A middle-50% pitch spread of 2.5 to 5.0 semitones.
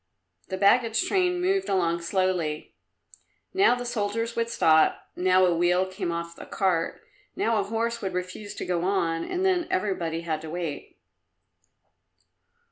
No: wide, 5.4 semitones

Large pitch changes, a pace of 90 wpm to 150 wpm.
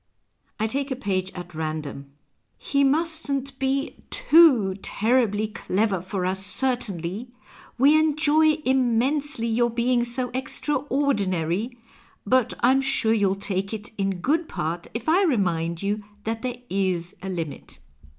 Yes: wide, 6.1 semitones; average, 140 wpm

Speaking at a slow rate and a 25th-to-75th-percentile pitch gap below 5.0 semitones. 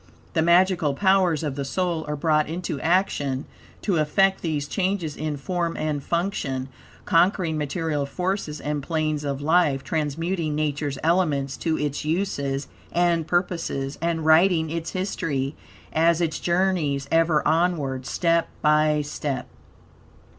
Yes: slow, 130 wpm; average, 3.0 semitones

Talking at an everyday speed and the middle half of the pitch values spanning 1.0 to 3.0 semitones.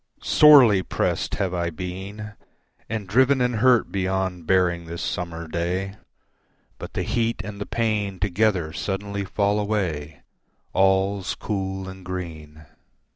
No: slow, 130 wpm; average, 2.7 semitones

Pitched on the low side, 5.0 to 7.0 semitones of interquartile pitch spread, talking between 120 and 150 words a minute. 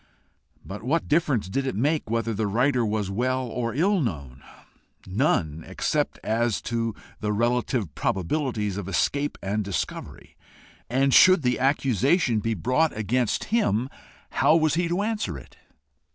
Yes: low, 120 Hz; average, 5.3 semitones; average, 145 wpm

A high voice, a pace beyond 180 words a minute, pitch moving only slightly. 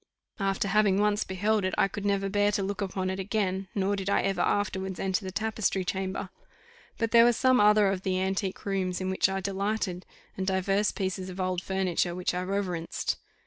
Yes: high, 195 Hz; average, 200 wpm; narrow, 1.5 semitones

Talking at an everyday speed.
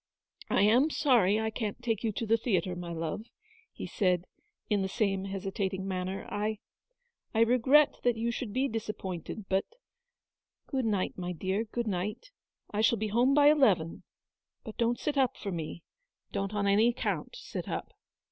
Yes: average, 185 wpm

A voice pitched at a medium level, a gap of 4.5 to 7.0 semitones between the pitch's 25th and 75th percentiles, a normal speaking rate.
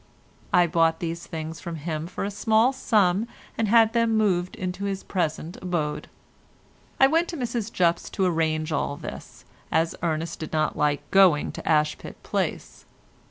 Yes: medium, 175 Hz; average, 4.8 semitones; average, 160 wpm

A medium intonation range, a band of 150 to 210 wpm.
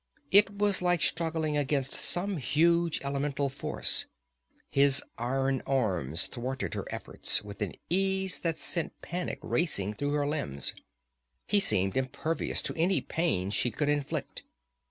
No: average, 4.7 semitones; slow, 135 wpm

